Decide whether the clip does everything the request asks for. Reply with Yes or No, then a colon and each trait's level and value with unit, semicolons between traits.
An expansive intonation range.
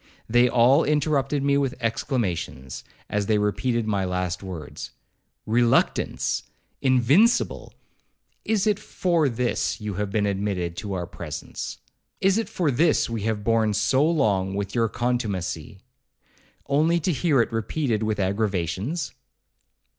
Yes: wide, 5.9 semitones